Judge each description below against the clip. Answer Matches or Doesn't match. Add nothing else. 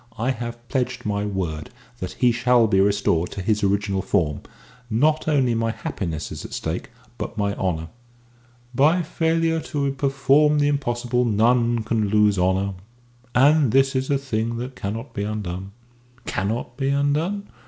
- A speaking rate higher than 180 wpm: Doesn't match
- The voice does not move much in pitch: Doesn't match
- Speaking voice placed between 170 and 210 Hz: Doesn't match